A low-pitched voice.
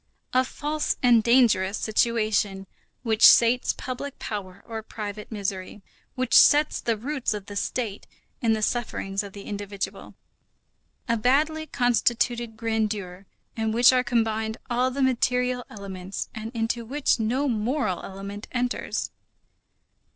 No: high, 225 Hz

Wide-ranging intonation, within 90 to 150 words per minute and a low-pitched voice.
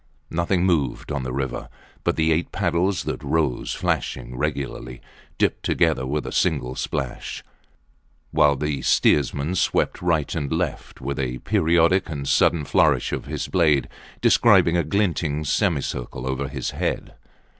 No: average, 3.8 semitones; average, 145 wpm; very low, 75 Hz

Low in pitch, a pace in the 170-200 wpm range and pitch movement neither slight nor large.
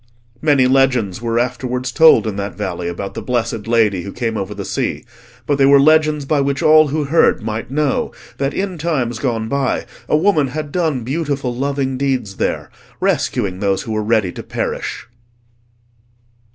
Yes: low, 130 Hz; average, 175 wpm; average, 4.5 semitones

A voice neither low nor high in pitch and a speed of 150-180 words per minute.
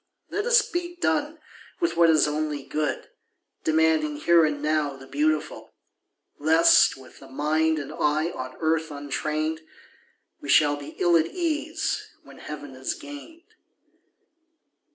No: medium, 155 Hz; slow, 135 wpm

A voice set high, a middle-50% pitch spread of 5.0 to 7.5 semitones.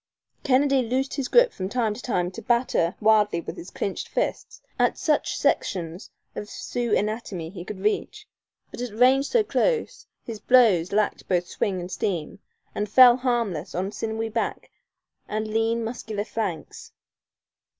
No: high, 220 Hz; average, 4.5 semitones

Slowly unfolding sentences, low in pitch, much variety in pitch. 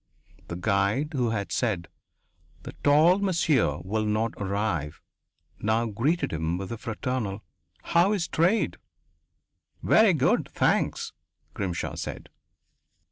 Yes: slow, 115 wpm; low, 110 Hz; wide, 7.7 semitones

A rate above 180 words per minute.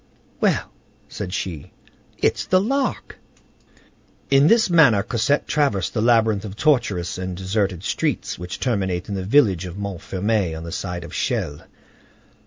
No: average, 145 wpm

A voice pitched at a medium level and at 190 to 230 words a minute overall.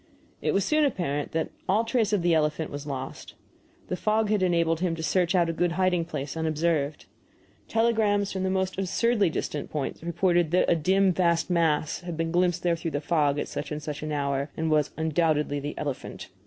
Yes: medium, 170 Hz; fast, 205 wpm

